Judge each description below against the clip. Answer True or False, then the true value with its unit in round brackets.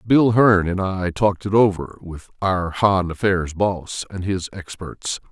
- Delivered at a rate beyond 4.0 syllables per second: False (3.9 syllables/s)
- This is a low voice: True (95 Hz)